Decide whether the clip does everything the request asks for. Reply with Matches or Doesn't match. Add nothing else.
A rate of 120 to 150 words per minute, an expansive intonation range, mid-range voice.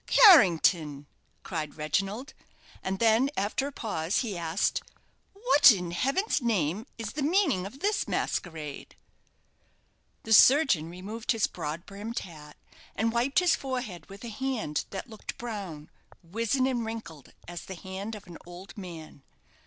Doesn't match